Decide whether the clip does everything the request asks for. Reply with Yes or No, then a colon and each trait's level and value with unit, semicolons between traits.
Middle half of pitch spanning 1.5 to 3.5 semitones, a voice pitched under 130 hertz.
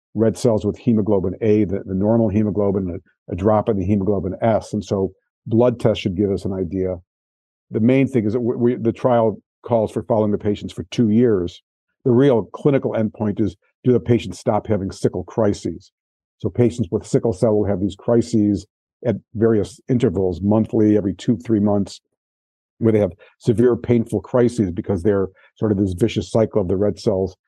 Yes: average, 2.8 semitones; low, 105 Hz